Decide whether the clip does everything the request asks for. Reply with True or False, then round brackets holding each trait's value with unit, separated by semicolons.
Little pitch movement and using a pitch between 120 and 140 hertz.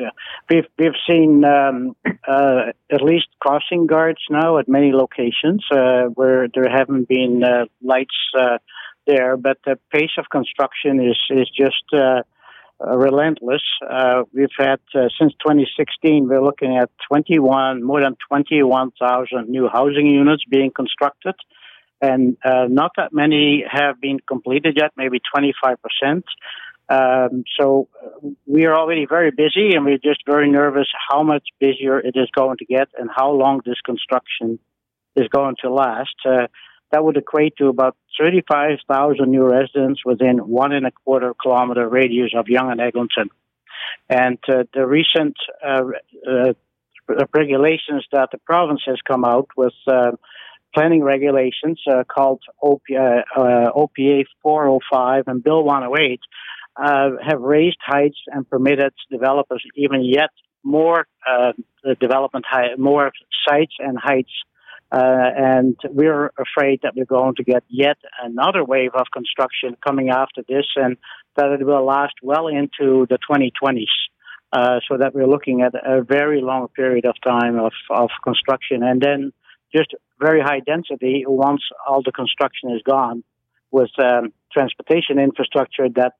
True (2.1 semitones; 135 Hz)